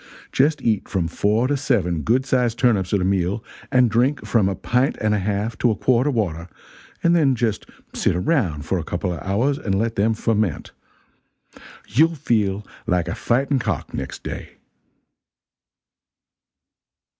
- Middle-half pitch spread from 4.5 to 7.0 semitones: Yes, average, 4.8 semitones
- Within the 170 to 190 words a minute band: No, average, 160 wpm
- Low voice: Yes, low, 110 Hz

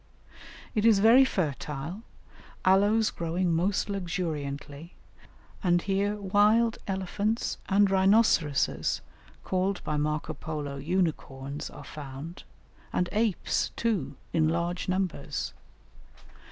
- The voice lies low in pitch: No, medium, 180 Hz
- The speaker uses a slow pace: Yes, slow, 100 wpm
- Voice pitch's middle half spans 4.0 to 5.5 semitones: Yes, average, 4.9 semitones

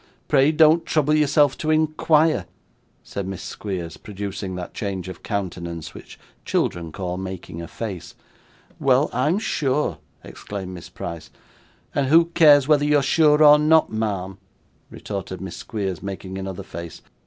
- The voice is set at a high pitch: No, low, 105 Hz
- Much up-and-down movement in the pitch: Yes, wide, 8.2 semitones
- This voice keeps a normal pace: Yes, average, 145 wpm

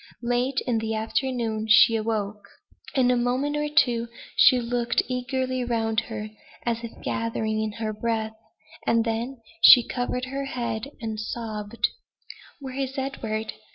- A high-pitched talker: Yes, high, 235 Hz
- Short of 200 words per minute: Yes, average, 145 wpm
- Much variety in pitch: No, narrow, 2.5 semitones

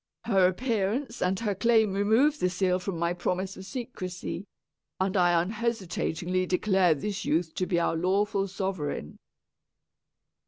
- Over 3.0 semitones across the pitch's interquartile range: No, narrow, 2.6 semitones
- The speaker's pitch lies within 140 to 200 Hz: Yes, high, 190 Hz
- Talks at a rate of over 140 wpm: No, slow, 135 wpm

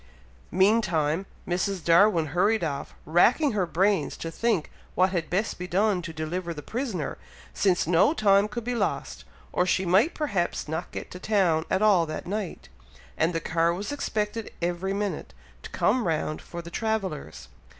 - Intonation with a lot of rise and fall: No, average, 4.0 semitones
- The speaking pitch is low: No, medium, 180 Hz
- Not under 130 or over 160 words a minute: No, average, 170 wpm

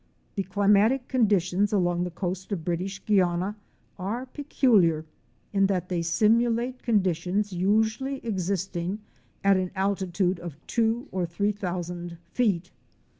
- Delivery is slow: Yes, slow, 125 wpm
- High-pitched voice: Yes, high, 195 Hz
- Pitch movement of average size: Yes, average, 3.2 semitones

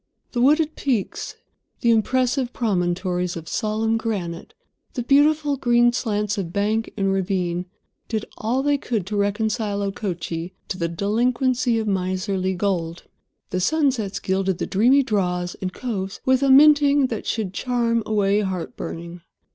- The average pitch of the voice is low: No, high, 210 Hz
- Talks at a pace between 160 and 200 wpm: No, average, 145 wpm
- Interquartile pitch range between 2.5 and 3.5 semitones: No, average, 4.7 semitones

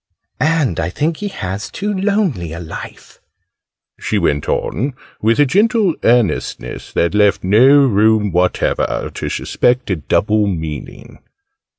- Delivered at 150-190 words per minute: No, slow, 135 wpm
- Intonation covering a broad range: Yes, wide, 8.7 semitones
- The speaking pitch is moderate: No, low, 110 Hz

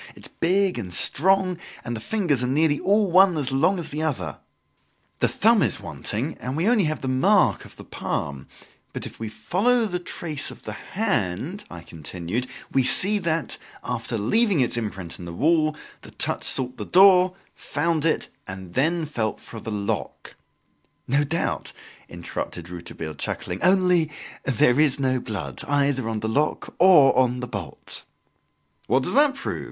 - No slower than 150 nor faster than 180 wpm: Yes, average, 175 wpm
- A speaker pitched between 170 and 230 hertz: No, medium, 145 Hz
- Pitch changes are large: Yes, wide, 8.1 semitones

